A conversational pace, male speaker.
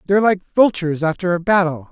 Yes: average, 190 wpm; male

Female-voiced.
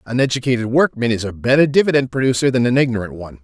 No: male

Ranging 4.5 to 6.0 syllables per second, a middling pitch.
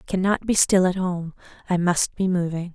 Yes: 5.4 syllables/s; medium, 180 Hz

